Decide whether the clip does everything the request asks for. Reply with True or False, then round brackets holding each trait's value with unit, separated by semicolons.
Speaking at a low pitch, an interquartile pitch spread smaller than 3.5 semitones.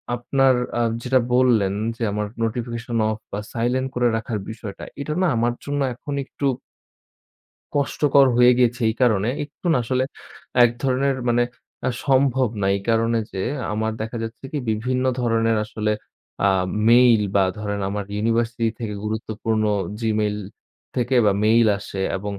True (115 Hz; 2.7 semitones)